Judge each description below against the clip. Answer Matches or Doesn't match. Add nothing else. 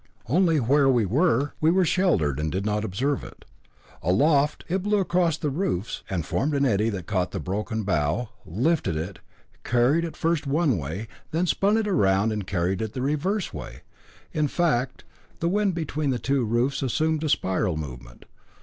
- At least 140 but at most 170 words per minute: Doesn't match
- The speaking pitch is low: Matches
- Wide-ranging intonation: Matches